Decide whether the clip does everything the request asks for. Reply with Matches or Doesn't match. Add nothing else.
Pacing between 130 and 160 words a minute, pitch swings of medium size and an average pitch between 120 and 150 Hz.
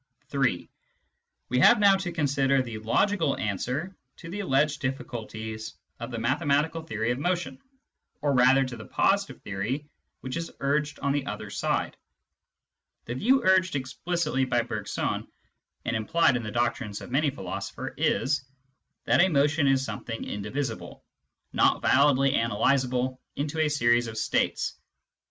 Matches